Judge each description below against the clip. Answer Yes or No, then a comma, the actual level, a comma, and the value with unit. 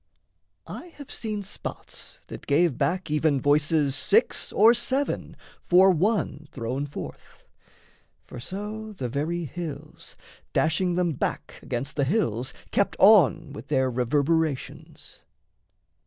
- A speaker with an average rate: No, slow, 120 wpm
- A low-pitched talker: No, medium, 160 Hz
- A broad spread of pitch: Yes, wide, 5.7 semitones